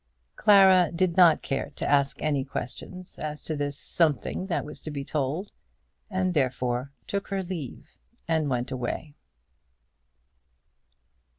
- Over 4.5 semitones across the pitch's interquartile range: Yes, average, 5.0 semitones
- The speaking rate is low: Yes, slow, 130 wpm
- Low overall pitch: No, medium, 155 Hz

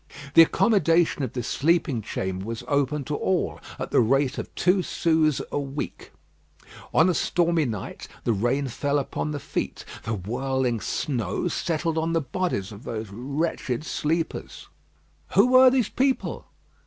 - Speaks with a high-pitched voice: No, medium, 145 Hz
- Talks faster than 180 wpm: No, average, 155 wpm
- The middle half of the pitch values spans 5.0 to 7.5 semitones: Yes, wide, 5.4 semitones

